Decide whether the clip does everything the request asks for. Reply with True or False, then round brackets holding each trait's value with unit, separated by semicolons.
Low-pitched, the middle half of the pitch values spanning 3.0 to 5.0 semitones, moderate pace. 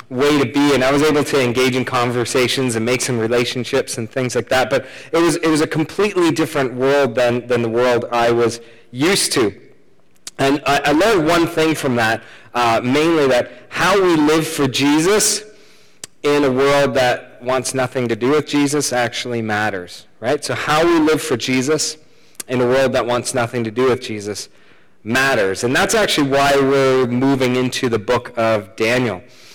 True (130 Hz; 3.5 semitones; 190 wpm)